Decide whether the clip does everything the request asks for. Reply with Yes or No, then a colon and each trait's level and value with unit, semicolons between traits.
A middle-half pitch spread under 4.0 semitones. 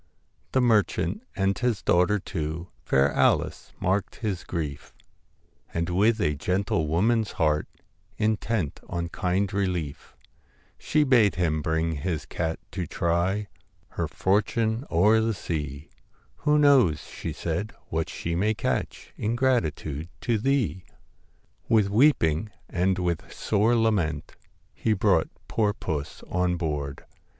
No: average, 5.2 semitones